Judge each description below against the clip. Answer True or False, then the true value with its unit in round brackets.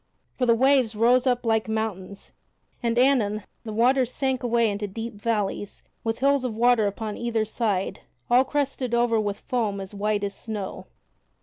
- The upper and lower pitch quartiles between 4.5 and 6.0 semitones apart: False (2.9 semitones)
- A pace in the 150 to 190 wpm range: True (170 wpm)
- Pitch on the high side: True (225 Hz)